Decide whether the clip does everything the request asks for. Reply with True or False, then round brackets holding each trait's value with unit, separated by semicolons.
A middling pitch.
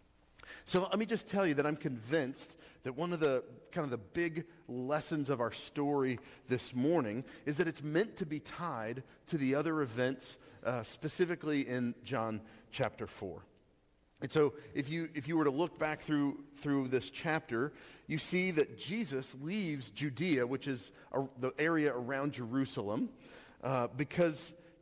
True (145 Hz)